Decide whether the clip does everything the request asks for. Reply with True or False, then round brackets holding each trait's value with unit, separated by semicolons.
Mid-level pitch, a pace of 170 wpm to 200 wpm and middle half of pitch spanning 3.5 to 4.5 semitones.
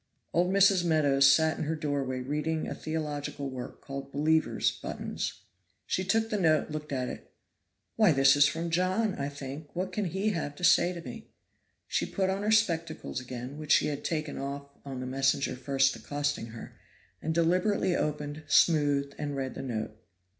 True (150 Hz; 180 wpm; 3.8 semitones)